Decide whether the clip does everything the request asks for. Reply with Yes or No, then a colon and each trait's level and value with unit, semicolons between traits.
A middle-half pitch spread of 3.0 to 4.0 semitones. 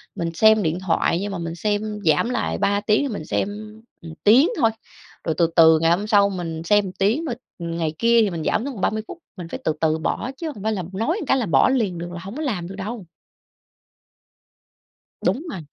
No: average, 4.7 semitones